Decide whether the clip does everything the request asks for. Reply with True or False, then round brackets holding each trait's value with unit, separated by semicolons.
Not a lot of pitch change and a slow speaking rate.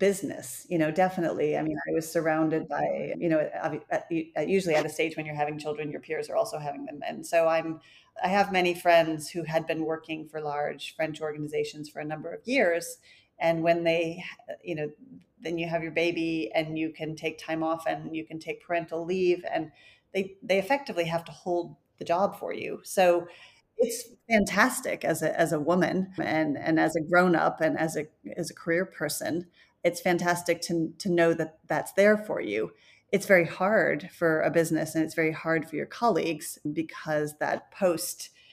False (2.3 semitones; 195 wpm)